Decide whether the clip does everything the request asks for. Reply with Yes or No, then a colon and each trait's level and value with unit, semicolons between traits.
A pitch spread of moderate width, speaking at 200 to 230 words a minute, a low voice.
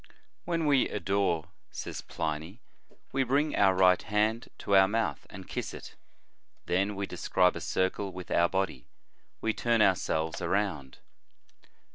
No: average, 3.7 semitones; average, 145 wpm; very low, 95 Hz